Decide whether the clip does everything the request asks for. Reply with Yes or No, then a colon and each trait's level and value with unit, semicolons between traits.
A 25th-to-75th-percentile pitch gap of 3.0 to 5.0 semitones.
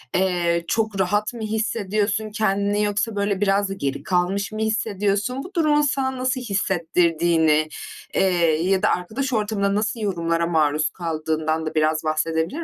Yes: average, 4.4 semitones